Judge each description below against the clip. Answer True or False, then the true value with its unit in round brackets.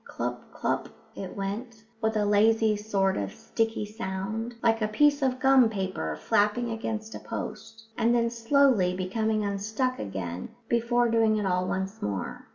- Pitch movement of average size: True (3.0 semitones)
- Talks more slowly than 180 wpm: True (160 wpm)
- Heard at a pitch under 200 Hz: False (220 Hz)